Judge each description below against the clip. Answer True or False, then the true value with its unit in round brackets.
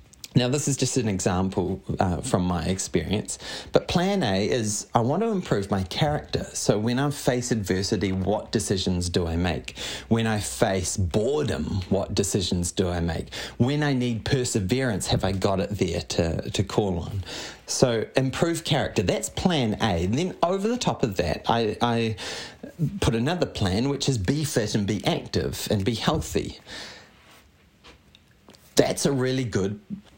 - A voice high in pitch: False (110 Hz)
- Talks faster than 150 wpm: True (165 wpm)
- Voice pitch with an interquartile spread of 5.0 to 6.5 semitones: True (5.6 semitones)